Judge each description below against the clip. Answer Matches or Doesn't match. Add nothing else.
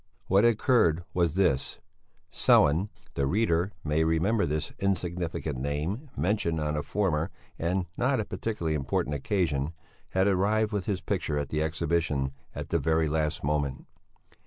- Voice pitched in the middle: Doesn't match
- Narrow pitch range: Doesn't match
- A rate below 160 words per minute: Matches